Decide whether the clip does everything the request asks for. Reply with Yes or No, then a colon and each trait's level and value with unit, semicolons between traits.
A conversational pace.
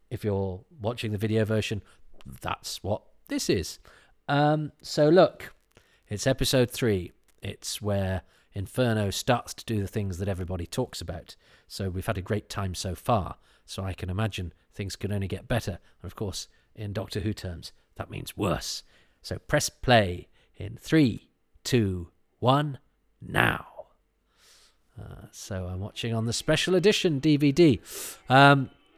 Yes: average, 150 wpm